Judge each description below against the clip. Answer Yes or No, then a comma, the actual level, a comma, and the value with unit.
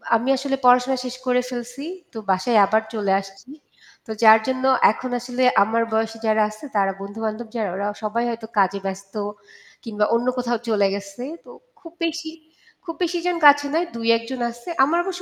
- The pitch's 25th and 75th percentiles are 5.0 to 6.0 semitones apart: No, average, 3.3 semitones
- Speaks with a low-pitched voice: No, high, 230 Hz